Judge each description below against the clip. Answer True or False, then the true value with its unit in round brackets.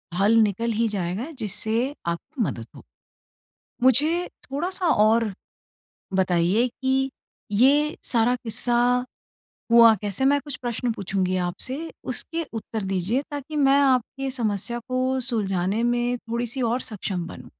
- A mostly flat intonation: False (4.4 semitones)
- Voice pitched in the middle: False (235 Hz)